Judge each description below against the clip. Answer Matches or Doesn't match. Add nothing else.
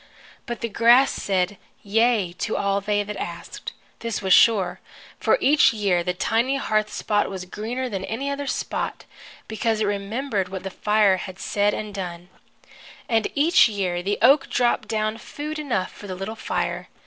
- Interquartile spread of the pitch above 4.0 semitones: Doesn't match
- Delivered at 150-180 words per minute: Matches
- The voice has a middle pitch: Doesn't match